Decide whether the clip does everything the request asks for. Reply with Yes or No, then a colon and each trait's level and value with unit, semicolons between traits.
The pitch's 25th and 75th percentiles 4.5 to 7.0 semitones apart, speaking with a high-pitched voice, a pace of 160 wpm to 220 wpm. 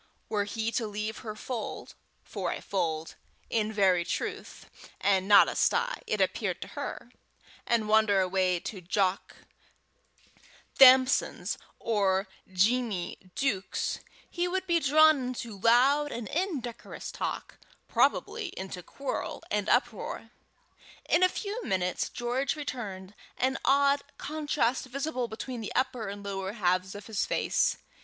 No: wide, 5.4 semitones; high, 225 Hz; slow, 135 wpm